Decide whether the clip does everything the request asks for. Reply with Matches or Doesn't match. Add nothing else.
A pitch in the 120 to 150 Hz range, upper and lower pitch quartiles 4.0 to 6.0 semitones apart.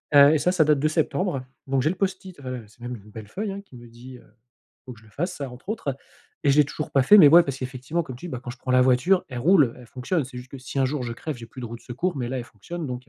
Matches